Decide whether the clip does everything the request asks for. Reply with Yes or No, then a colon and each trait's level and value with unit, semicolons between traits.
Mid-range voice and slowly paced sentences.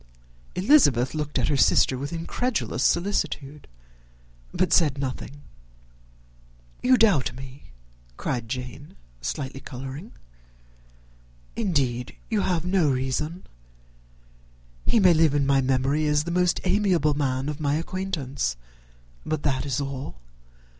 Yes: medium, 145 Hz; slow, 120 wpm